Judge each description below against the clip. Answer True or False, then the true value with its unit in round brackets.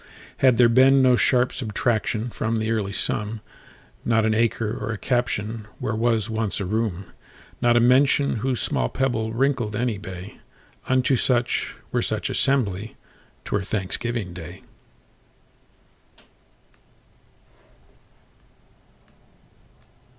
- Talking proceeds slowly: True (95 wpm)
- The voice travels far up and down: False (2.7 semitones)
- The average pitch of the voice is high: False (115 Hz)